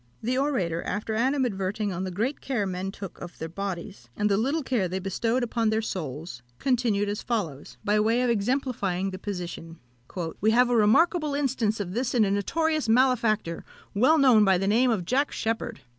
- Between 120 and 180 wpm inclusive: No, average, 190 wpm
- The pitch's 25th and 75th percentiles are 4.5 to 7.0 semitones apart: Yes, average, 4.8 semitones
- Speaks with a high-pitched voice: Yes, high, 215 Hz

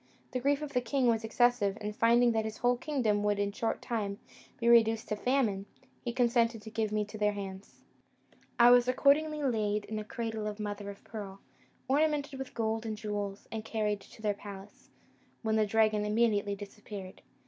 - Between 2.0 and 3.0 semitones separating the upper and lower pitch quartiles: Yes, narrow, 2.6 semitones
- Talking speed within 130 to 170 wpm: No, average, 190 wpm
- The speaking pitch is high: Yes, high, 220 Hz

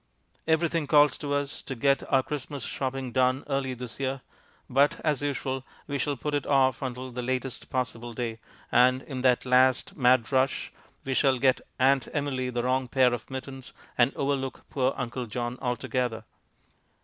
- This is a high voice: No, low, 130 Hz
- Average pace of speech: Yes, average, 170 wpm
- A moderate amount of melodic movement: No, narrow, 1.6 semitones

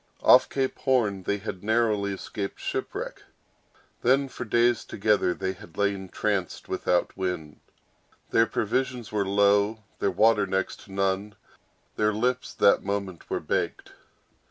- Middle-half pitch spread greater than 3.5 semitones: No, average, 2.8 semitones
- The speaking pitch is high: No, low, 100 Hz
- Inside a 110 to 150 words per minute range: Yes, slow, 135 wpm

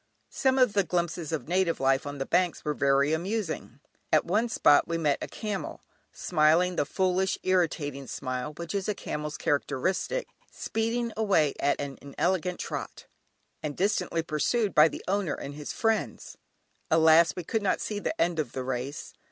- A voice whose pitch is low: No, medium, 165 Hz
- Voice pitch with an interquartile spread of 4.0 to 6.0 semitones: Yes, average, 4.9 semitones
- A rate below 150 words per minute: No, average, 170 wpm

